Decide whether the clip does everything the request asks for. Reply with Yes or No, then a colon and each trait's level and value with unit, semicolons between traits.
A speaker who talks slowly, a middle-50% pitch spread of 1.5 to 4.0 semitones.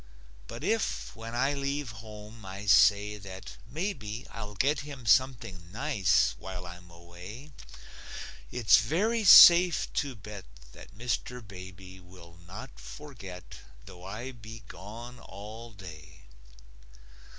No: slow, 120 wpm; average, 5.2 semitones